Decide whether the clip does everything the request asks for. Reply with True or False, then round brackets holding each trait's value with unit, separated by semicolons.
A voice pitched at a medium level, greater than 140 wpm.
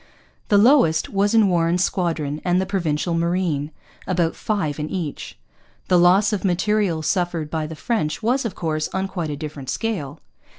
True (175 Hz; 170 wpm)